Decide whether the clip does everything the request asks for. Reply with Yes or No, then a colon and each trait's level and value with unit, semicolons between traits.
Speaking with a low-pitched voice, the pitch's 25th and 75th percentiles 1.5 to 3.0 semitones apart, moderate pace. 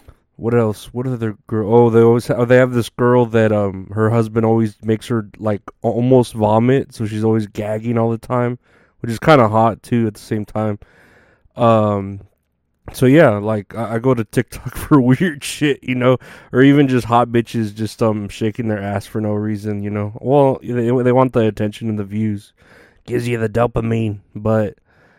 Yes: low, 115 Hz; narrow, 2.5 semitones; average, 195 wpm